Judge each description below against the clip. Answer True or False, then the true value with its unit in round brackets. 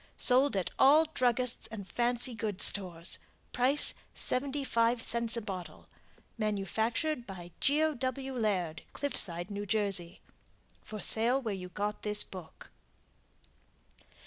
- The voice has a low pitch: False (225 Hz)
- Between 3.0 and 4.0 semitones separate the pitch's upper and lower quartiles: False (4.5 semitones)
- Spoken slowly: True (115 wpm)